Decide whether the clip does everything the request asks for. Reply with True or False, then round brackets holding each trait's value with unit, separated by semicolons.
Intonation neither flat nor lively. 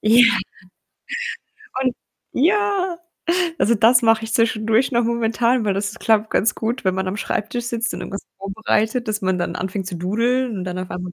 True (3.4 semitones)